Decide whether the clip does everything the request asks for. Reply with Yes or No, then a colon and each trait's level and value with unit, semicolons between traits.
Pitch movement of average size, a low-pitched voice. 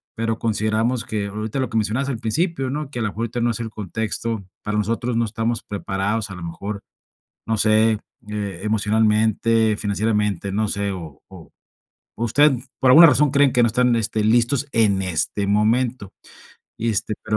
No: narrow, 2.2 semitones; low, 110 Hz